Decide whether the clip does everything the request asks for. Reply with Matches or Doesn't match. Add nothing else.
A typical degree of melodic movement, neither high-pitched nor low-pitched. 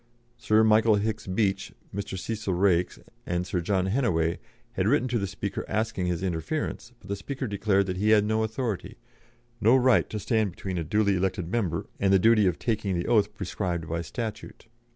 Doesn't match